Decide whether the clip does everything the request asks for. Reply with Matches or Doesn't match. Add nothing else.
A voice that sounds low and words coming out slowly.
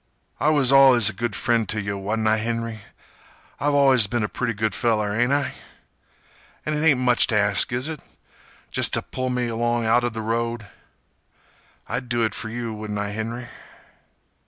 Doesn't match